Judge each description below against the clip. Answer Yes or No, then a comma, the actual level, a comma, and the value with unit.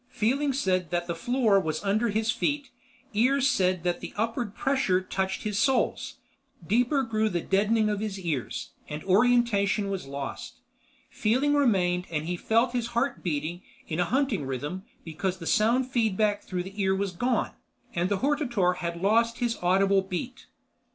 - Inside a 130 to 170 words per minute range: Yes, average, 165 wpm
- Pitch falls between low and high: No, high, 205 Hz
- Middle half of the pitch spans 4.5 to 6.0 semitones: Yes, average, 5.0 semitones